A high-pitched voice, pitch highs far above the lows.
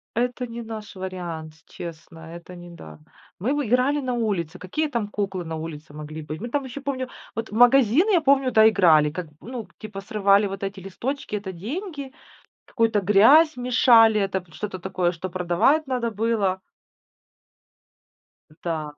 Yes: high, 210 Hz; wide, 5.9 semitones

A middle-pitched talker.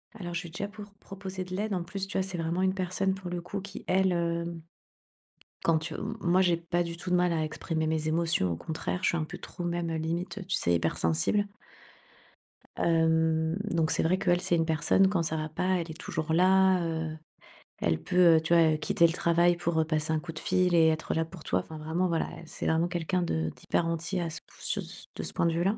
Yes: medium, 170 Hz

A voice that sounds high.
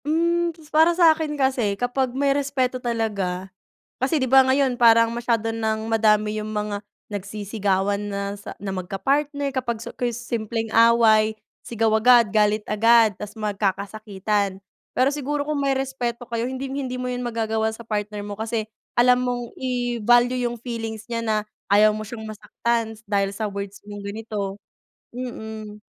Yes: high, 225 Hz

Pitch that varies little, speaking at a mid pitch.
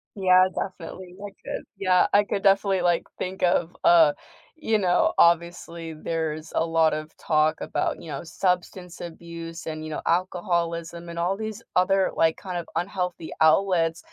Yes: narrow, 2.1 semitones; medium, 175 Hz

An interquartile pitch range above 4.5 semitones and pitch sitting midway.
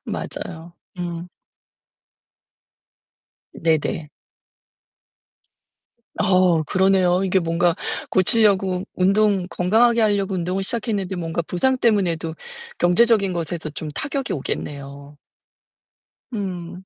No: average, 2.9 semitones; medium, 180 Hz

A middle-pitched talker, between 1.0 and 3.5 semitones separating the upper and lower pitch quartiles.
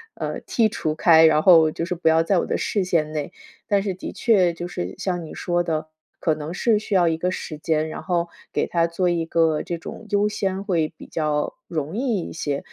Yes: medium, 170 Hz; average, 2.8 semitones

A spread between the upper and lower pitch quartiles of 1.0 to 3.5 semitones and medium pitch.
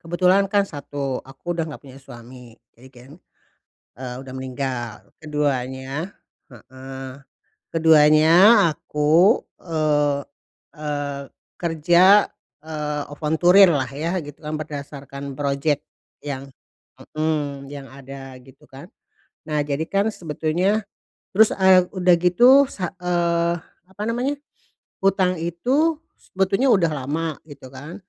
No: average, 4.4 semitones; medium, 150 Hz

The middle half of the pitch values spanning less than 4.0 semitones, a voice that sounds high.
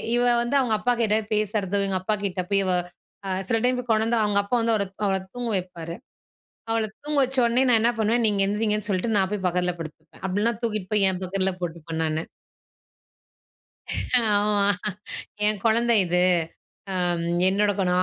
Yes: average, 3.5 semitones; high, 205 Hz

